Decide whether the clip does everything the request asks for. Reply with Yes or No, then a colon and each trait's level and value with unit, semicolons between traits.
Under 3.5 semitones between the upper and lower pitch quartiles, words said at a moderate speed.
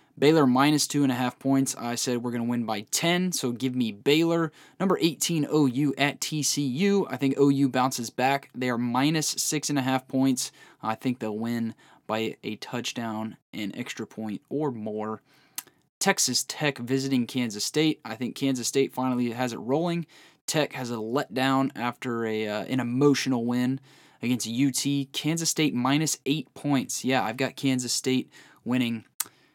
Yes: average, 2.9 semitones; average, 175 wpm